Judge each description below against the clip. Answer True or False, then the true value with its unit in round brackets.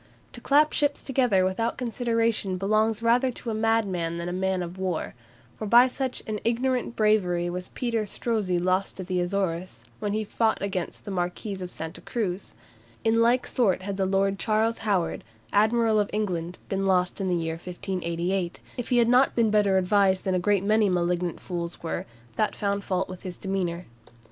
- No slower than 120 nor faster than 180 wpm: False (190 wpm)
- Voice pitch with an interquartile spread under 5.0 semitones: True (3.7 semitones)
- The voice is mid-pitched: False (195 Hz)